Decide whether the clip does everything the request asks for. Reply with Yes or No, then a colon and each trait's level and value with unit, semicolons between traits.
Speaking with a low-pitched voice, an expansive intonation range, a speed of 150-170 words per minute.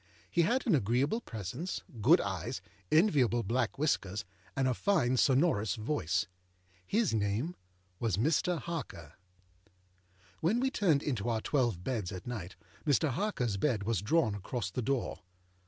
No: low, 125 Hz; wide, 7.3 semitones; average, 140 wpm